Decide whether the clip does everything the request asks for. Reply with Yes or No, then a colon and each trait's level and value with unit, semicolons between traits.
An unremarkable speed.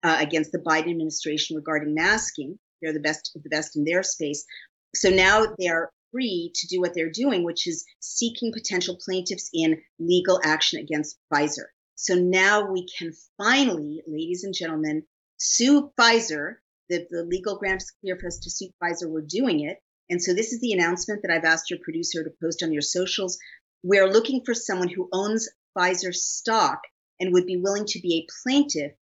Yes: average, 190 wpm